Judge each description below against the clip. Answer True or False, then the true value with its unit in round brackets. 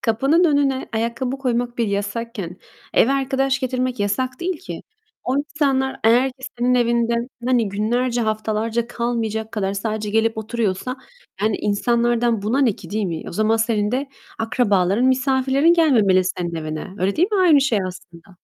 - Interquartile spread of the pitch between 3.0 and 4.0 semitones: True (3.6 semitones)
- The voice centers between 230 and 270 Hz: True (235 Hz)